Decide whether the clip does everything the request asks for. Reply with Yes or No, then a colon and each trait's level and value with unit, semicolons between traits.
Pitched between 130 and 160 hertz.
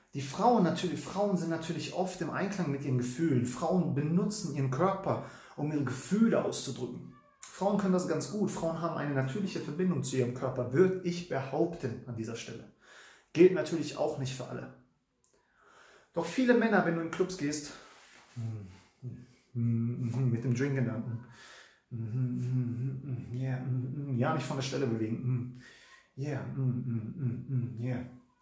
Yes: low, 135 Hz